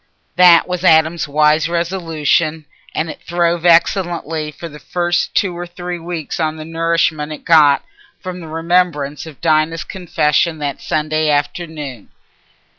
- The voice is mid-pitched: Yes, medium, 165 Hz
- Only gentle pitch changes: Yes, narrow, 2.1 semitones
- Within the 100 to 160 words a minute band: Yes, average, 140 wpm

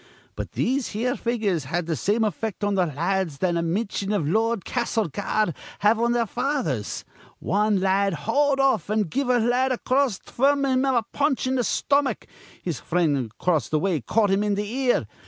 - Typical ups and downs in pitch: No, wide, 5.7 semitones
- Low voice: No, high, 210 Hz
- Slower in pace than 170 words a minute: No, average, 195 wpm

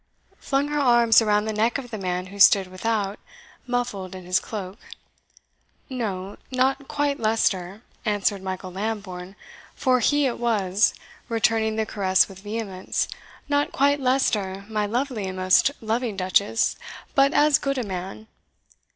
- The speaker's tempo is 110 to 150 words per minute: Yes, average, 145 wpm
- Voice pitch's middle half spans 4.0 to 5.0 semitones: Yes, average, 4.4 semitones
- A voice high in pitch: Yes, high, 215 Hz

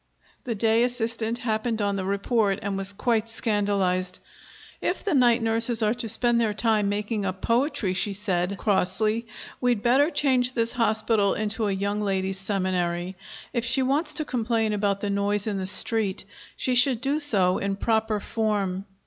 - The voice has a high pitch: Yes, high, 215 Hz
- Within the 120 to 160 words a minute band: No, average, 170 wpm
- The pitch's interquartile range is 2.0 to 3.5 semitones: Yes, average, 3.0 semitones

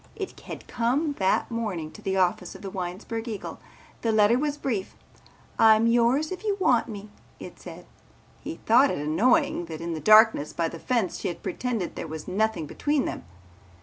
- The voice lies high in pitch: Yes, high, 220 Hz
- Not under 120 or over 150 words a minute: No, average, 185 wpm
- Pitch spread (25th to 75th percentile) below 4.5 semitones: No, average, 5.3 semitones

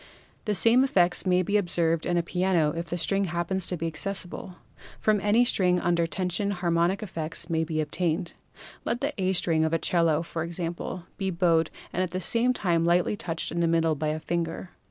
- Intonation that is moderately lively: No, narrow, 2.3 semitones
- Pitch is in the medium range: Yes, medium, 175 Hz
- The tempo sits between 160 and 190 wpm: No, fast, 205 wpm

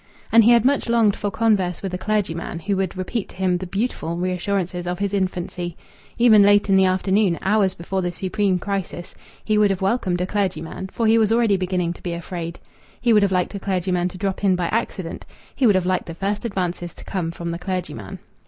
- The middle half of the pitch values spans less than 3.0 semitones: Yes, narrow, 2.4 semitones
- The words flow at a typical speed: No, fast, 220 wpm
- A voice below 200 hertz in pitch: Yes, high, 190 Hz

